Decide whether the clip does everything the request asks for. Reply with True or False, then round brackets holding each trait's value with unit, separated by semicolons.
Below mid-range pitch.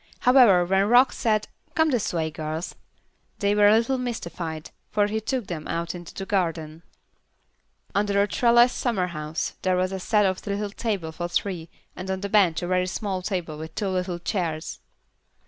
False (190 Hz)